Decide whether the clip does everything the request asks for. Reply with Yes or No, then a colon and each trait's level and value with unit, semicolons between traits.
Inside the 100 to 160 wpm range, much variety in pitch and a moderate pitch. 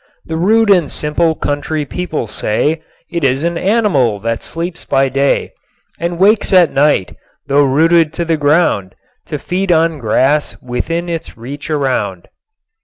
No: average, 150 wpm; average, 4.0 semitones; medium, 155 Hz